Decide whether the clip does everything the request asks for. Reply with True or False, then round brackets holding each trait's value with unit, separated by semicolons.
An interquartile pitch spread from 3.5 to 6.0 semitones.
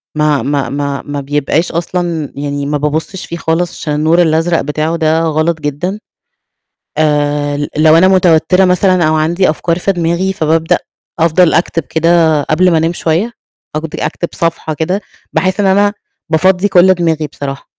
False (2.7 semitones)